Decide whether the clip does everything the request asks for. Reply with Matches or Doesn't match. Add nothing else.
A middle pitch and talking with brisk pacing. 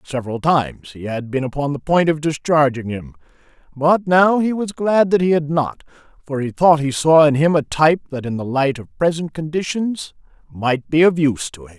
Matches